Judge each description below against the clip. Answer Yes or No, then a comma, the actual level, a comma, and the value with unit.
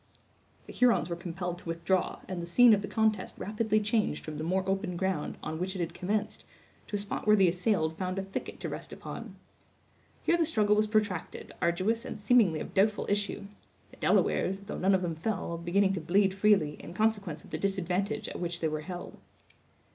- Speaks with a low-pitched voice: No, high, 190 Hz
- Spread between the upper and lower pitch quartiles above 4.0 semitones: No, average, 3.3 semitones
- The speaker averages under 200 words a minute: No, fast, 205 wpm